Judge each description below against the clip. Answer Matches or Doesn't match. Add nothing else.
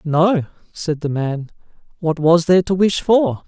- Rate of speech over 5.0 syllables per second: Doesn't match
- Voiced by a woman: Doesn't match